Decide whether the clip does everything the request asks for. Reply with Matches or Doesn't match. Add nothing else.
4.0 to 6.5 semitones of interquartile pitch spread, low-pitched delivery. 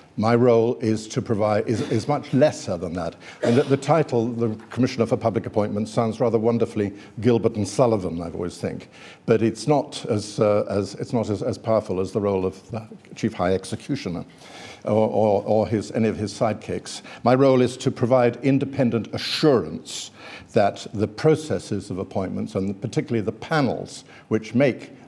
Doesn't match